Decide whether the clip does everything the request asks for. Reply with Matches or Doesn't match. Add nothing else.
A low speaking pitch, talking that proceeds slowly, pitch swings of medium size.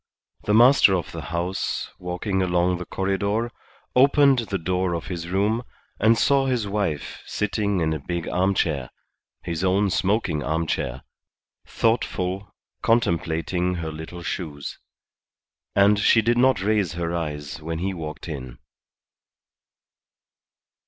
Matches